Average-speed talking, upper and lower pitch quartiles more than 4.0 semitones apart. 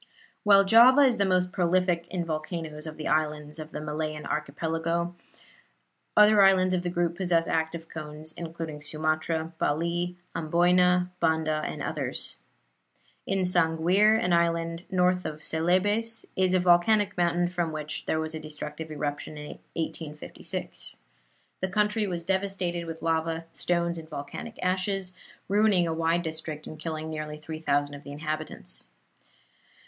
No: average, 145 wpm; narrow, 2.6 semitones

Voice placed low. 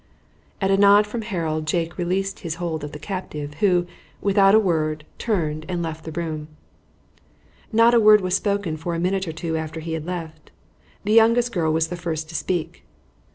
No: medium, 175 Hz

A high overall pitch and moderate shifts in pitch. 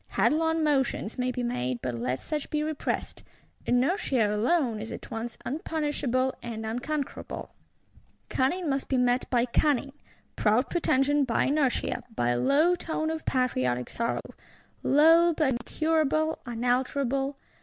Yes: very high, 265 Hz; average, 4.4 semitones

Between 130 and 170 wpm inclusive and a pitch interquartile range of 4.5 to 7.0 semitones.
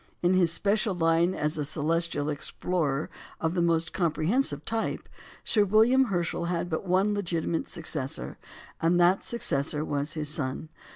No: average, 150 wpm; average, 3.3 semitones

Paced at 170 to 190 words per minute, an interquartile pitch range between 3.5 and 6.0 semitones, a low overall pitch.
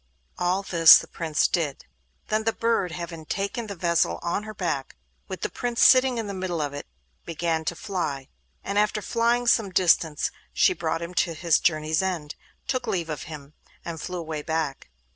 No: average, 180 wpm; average, 4.2 semitones; medium, 170 Hz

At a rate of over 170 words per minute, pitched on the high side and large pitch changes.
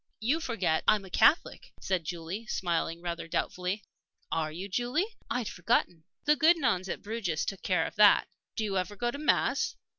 Yes: average, 180 wpm; high, 195 Hz; wide, 5.7 semitones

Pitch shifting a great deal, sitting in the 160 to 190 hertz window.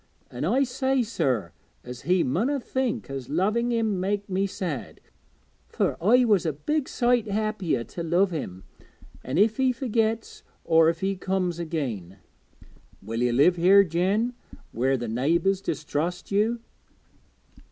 Yes: wide, 6.8 semitones; medium, 185 Hz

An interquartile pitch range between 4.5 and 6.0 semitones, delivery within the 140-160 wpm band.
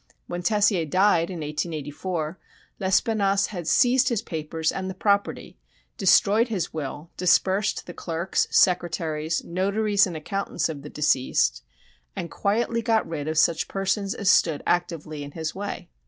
No: average, 4.1 semitones; average, 145 wpm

